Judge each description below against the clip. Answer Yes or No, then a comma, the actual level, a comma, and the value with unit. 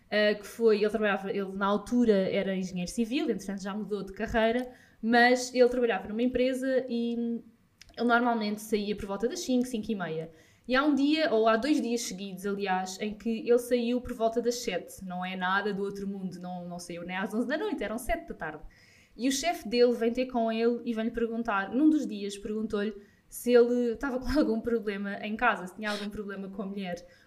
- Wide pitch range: No, average, 3.3 semitones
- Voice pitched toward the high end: Yes, high, 225 Hz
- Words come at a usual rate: No, fast, 215 wpm